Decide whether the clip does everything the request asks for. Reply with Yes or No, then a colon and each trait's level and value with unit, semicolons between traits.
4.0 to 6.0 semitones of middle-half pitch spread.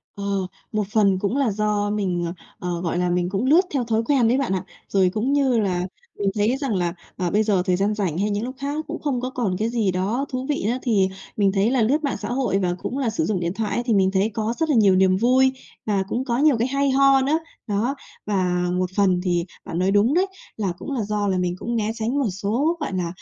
Yes: average, 5.2 semitones